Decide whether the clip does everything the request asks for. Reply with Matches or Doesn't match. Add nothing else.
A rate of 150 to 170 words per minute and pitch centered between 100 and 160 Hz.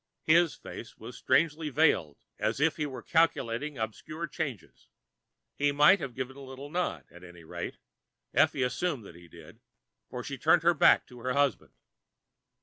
Matches